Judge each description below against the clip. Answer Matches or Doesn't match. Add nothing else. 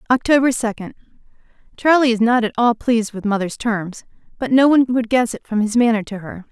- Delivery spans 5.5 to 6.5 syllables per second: Matches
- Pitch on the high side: Matches